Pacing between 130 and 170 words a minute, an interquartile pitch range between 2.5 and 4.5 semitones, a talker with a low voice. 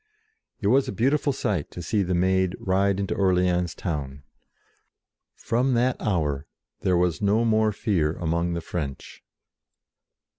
Yes: average, 140 wpm; average, 4.0 semitones; very low, 95 Hz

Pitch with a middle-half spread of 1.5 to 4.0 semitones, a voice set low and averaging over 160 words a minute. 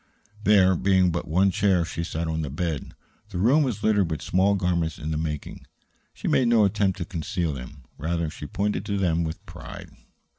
Yes: average, 3.7 semitones; very low, 90 Hz; average, 195 wpm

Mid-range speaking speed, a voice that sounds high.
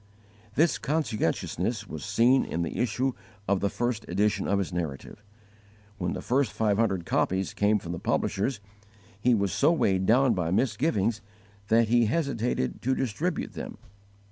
No: average, 155 wpm; low, 105 Hz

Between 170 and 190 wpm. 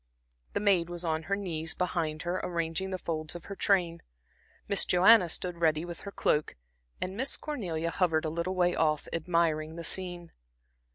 Yes: average, 175 wpm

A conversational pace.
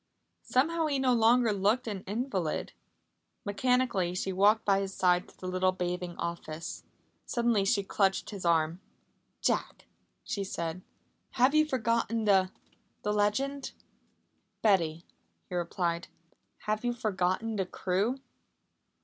No: slow, 125 wpm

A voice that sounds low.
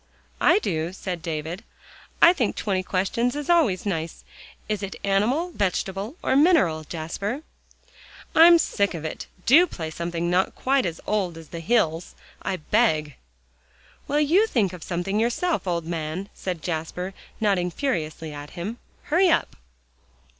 No: high, 190 Hz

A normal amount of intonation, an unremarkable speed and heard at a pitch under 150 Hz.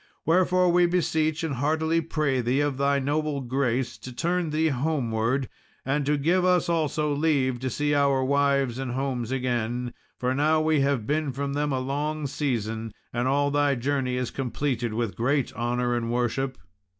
Yes: average, 3.3 semitones; average, 175 wpm; medium, 140 Hz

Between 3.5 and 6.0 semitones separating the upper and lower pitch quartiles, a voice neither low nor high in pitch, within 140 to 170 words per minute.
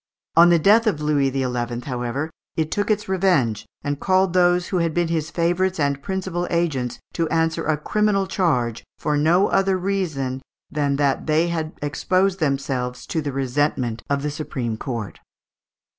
Yes: average, 4.7 semitones; medium, 155 Hz; average, 165 wpm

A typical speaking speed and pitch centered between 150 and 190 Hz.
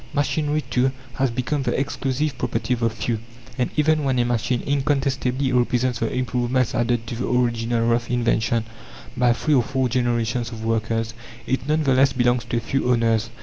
No: average, 185 wpm; low, 125 Hz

